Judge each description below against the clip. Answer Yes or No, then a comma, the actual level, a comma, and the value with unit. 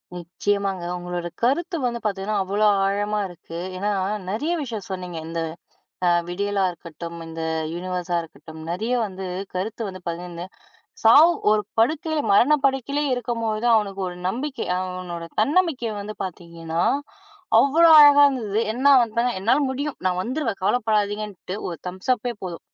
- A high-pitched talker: Yes, high, 205 Hz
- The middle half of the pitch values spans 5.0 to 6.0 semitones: Yes, average, 5.3 semitones